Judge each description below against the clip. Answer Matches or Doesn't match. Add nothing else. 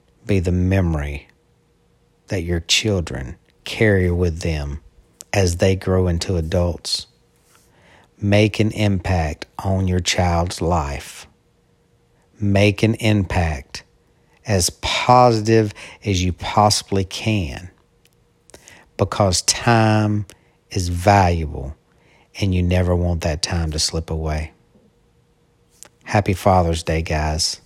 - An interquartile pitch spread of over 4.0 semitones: Doesn't match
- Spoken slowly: Matches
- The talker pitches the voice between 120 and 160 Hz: Doesn't match